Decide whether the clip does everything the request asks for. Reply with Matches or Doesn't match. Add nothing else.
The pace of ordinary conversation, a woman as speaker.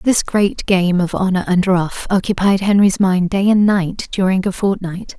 Matches